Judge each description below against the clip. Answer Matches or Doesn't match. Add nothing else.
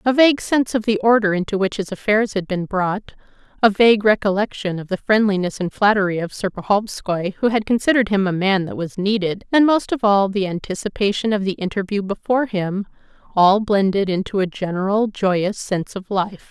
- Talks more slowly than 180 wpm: Doesn't match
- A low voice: Doesn't match